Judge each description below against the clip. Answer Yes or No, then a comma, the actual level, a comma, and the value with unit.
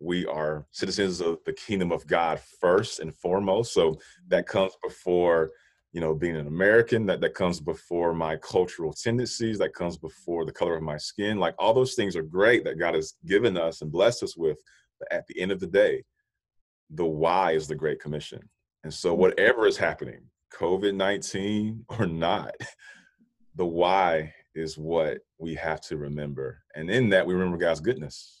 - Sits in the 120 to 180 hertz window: No, very low, 90 Hz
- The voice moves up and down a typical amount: No, wide, 7.1 semitones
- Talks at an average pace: Yes, average, 185 wpm